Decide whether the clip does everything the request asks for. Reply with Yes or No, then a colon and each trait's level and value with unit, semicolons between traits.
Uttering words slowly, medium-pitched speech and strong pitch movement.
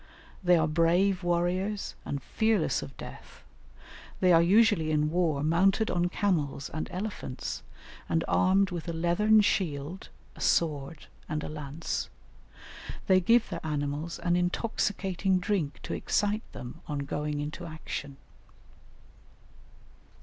No: slow, 130 wpm; medium, 170 Hz; average, 3.9 semitones